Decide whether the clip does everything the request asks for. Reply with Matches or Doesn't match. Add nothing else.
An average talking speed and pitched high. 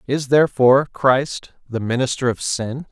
Doesn't match